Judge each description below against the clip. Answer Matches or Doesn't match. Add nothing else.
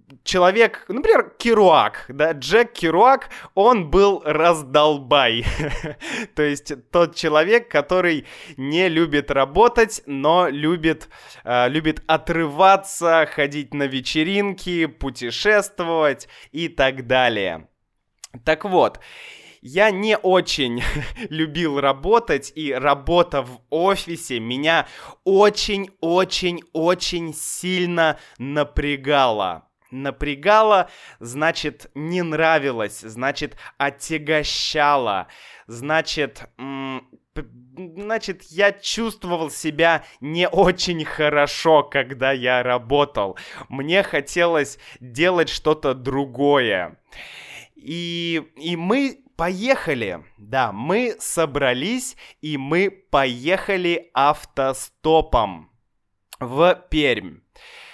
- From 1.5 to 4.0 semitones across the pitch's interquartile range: Doesn't match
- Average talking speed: Doesn't match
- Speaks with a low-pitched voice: Doesn't match